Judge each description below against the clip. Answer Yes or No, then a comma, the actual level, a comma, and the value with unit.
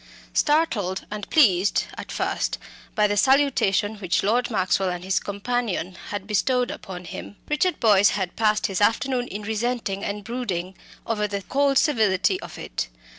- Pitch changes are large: No, average, 4.2 semitones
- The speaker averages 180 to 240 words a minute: No, average, 155 wpm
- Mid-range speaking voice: No, high, 210 Hz